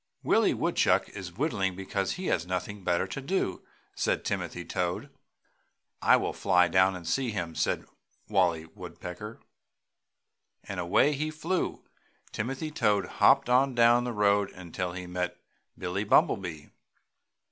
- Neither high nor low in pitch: No, very low, 95 Hz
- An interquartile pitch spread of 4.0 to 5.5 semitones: Yes, average, 5.2 semitones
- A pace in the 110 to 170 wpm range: Yes, slow, 135 wpm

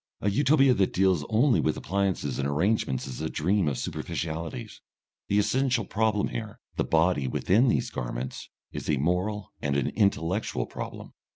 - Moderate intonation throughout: No, wide, 6.4 semitones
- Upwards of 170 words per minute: No, average, 160 wpm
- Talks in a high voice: No, very low, 95 Hz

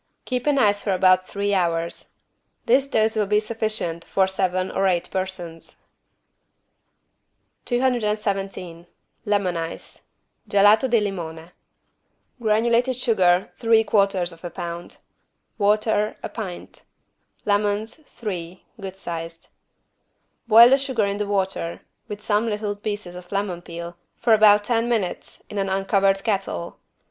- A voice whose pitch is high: Yes, high, 200 Hz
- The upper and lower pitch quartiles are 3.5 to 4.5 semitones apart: No, average, 3.1 semitones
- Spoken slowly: Yes, slow, 120 wpm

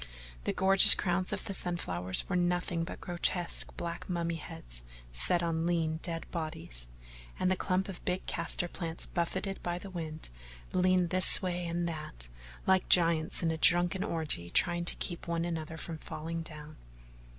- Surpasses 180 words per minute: No, average, 170 wpm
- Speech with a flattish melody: Yes, narrow, 1.8 semitones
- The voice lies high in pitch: No, medium, 170 Hz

